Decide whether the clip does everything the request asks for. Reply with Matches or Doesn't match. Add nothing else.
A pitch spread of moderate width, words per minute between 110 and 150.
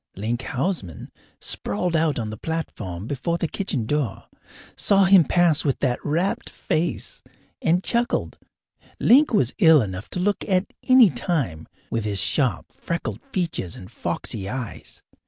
Doesn't match